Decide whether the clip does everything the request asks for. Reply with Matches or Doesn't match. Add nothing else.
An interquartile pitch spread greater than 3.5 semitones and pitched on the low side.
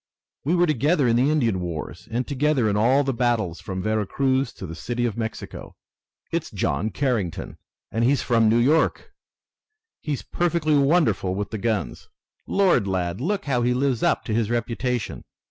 Matches